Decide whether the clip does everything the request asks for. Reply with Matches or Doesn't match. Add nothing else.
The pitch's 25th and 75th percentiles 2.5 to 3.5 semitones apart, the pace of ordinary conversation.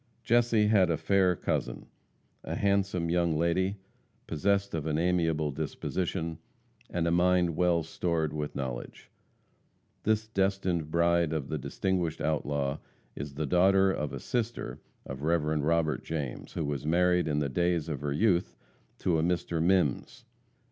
Matches